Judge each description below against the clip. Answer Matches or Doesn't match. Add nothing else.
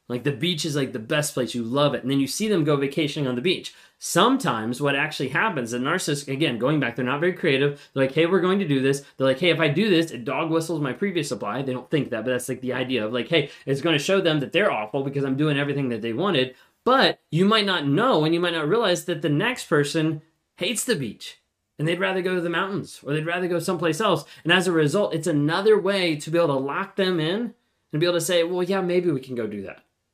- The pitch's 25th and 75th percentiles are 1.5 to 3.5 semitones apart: Doesn't match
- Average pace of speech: Doesn't match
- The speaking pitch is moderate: Matches